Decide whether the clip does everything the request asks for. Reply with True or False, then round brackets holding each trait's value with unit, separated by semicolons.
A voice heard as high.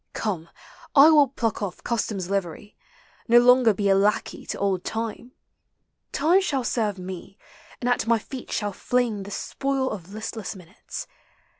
True (220 Hz)